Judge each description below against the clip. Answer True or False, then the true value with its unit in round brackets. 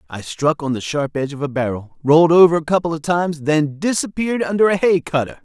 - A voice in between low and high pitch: True (160 Hz)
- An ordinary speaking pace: False (230 wpm)